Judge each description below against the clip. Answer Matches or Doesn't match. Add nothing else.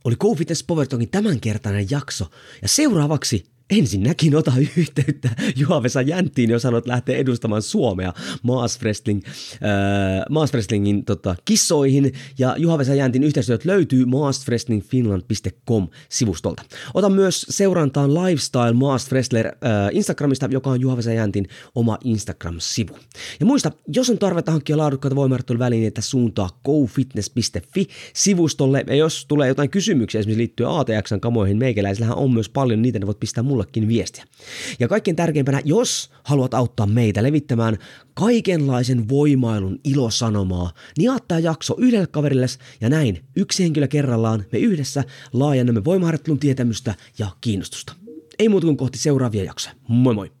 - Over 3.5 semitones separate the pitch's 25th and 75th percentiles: Matches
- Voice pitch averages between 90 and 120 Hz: Doesn't match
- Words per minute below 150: Matches